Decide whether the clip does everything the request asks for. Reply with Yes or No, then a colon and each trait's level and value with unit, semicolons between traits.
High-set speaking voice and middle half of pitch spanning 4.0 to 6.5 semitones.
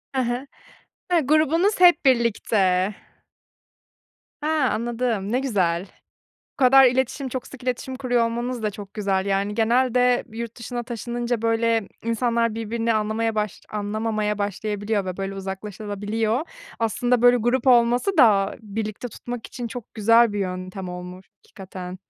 No: high, 230 Hz; average, 3.1 semitones